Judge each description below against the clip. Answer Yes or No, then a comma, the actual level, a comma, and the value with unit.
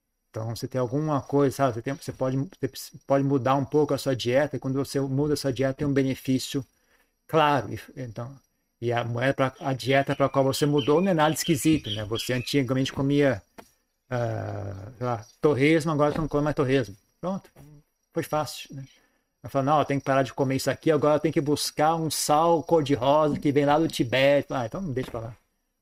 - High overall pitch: No, medium, 140 Hz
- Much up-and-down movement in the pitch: No, narrow, 2.4 semitones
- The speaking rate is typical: No, fast, 215 wpm